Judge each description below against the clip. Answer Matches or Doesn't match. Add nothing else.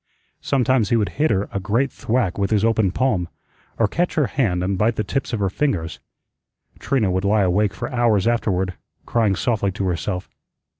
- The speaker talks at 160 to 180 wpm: Doesn't match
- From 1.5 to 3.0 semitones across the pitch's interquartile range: Doesn't match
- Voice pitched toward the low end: Matches